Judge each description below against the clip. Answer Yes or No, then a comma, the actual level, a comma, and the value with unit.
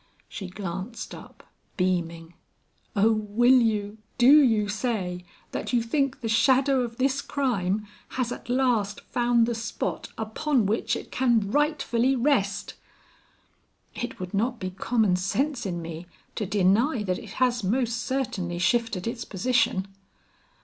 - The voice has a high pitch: Yes, high, 225 Hz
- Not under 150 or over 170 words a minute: No, average, 140 wpm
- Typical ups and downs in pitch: Yes, average, 4.3 semitones